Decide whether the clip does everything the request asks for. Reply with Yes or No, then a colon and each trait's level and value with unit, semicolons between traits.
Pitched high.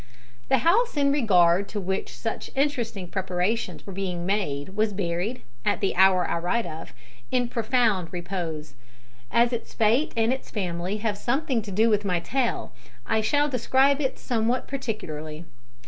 Yes: high, 210 Hz